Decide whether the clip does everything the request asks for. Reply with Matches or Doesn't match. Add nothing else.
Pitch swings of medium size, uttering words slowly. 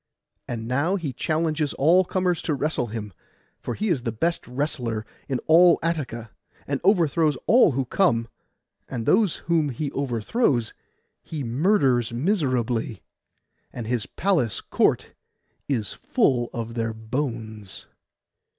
Doesn't match